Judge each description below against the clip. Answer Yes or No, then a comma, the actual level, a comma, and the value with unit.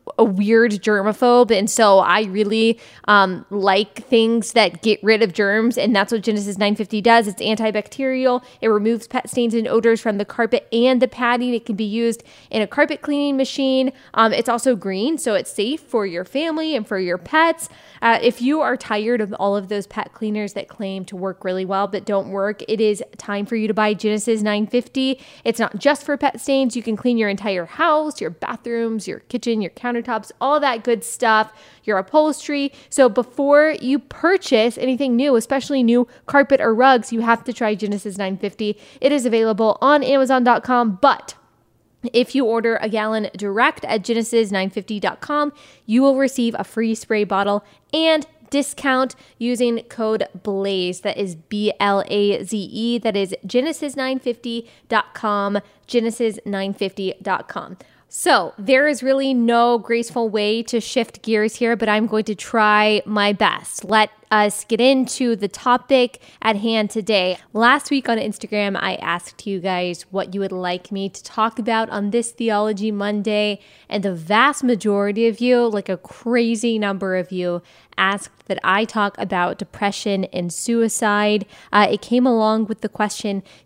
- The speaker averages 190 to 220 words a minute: No, average, 175 wpm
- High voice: Yes, high, 225 Hz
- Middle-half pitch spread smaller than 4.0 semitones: Yes, average, 3.1 semitones